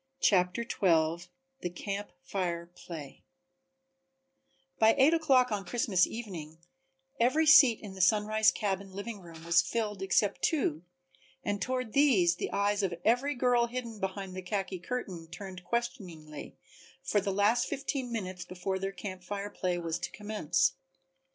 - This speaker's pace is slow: No, average, 145 wpm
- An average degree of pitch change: Yes, average, 4.6 semitones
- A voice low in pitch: No, high, 200 Hz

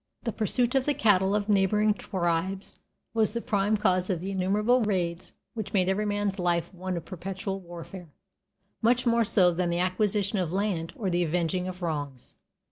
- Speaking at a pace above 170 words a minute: Yes, average, 180 wpm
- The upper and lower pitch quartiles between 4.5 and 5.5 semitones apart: No, average, 2.9 semitones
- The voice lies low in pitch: No, high, 190 Hz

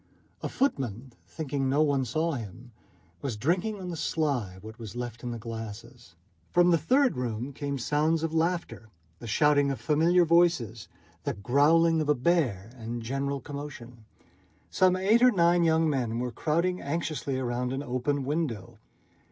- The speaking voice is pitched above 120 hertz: Yes, medium, 140 Hz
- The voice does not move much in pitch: No, wide, 5.5 semitones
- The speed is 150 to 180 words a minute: Yes, average, 160 wpm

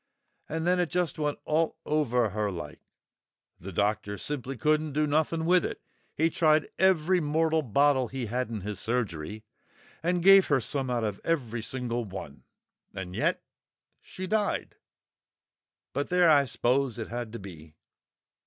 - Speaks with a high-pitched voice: No, low, 135 Hz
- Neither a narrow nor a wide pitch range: No, wide, 6.5 semitones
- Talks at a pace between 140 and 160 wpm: Yes, average, 155 wpm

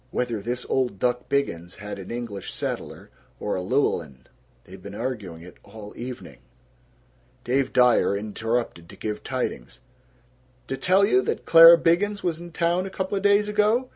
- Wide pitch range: Yes, wide, 8.9 semitones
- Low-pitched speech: Yes, low, 125 Hz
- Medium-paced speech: Yes, average, 155 wpm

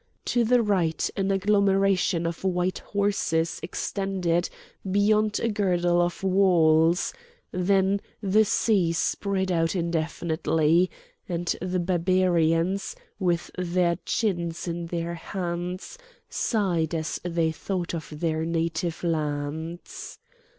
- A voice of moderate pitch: Yes, medium, 175 Hz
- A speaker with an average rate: No, slow, 110 wpm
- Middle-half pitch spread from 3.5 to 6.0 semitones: No, narrow, 2.6 semitones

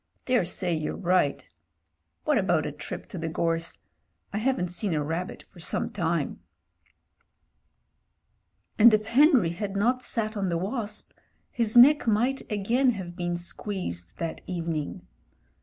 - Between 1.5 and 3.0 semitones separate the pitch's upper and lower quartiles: No, average, 5.1 semitones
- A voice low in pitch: No, high, 190 Hz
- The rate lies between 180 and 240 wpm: No, average, 140 wpm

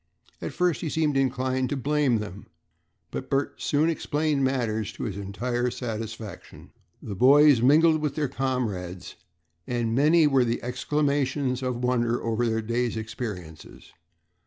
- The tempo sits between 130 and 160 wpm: Yes, average, 140 wpm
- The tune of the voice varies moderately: Yes, average, 4.2 semitones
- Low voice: Yes, low, 125 Hz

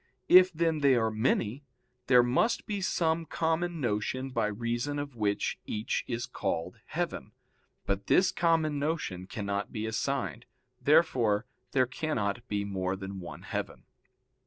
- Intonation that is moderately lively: No, wide, 6.9 semitones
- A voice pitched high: No, low, 120 Hz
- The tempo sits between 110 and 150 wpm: Yes, average, 140 wpm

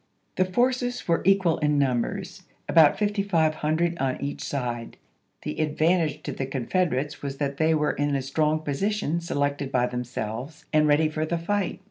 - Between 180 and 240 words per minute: No, average, 160 wpm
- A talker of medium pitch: Yes, medium, 155 Hz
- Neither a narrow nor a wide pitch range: Yes, average, 3.7 semitones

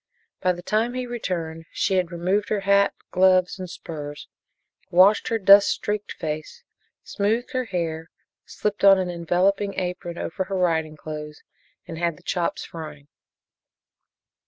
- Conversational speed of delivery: Yes, average, 145 wpm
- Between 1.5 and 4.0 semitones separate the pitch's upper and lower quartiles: Yes, average, 3.4 semitones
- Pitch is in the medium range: Yes, medium, 180 Hz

